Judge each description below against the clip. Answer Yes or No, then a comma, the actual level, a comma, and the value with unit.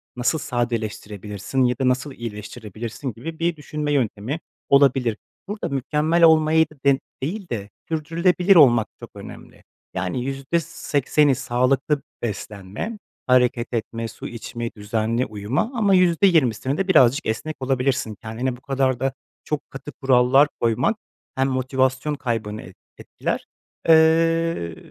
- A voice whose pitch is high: No, low, 130 Hz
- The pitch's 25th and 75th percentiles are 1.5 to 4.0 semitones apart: No, average, 4.8 semitones